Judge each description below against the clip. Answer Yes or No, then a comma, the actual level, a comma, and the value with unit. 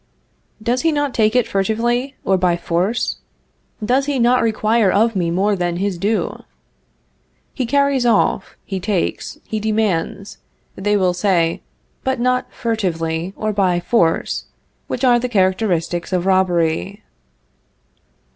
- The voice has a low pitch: No, high, 205 Hz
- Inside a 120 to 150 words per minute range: Yes, slow, 135 wpm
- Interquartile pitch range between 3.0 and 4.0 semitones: No, average, 4.8 semitones